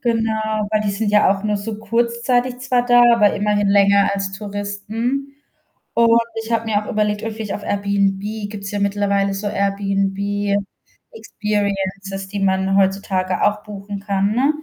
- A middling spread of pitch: No, narrow, 1.7 semitones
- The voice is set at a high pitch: Yes, high, 205 Hz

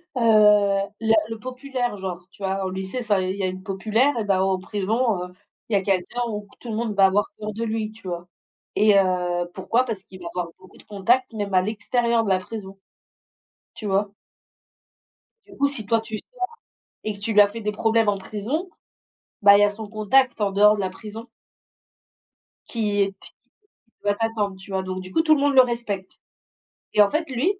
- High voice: Yes, high, 210 Hz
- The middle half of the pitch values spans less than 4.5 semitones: Yes, average, 2.9 semitones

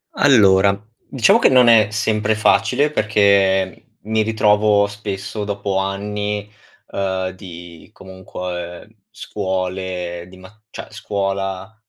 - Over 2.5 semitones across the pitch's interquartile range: No, narrow, 2.2 semitones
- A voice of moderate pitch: No, low, 100 Hz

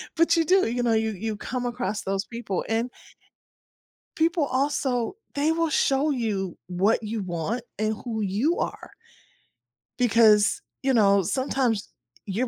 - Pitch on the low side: No, high, 230 Hz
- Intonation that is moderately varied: Yes, average, 4.3 semitones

